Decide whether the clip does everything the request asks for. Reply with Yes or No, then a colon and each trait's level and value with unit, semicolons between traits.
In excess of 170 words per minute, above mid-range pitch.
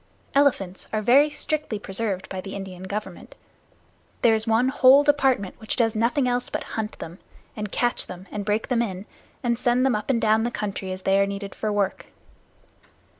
Yes: average, 190 wpm; high, 220 Hz